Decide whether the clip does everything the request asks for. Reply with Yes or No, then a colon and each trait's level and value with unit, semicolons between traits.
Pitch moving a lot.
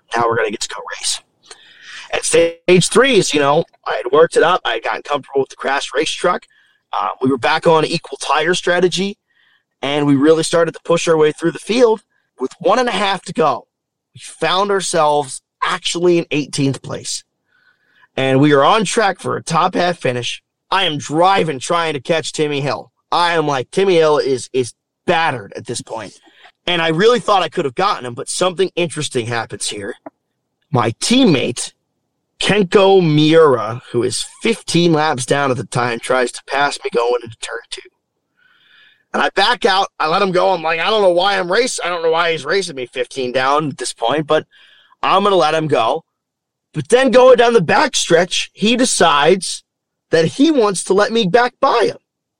Yes: wide, 6.0 semitones